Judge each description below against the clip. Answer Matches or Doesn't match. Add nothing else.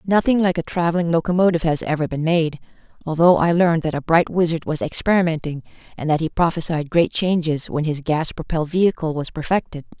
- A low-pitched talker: Doesn't match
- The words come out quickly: Doesn't match